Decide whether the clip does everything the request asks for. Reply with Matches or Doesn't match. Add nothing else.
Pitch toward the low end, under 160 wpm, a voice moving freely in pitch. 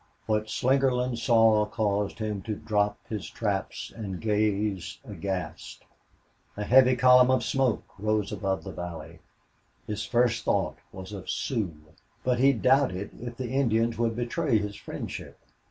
Doesn't match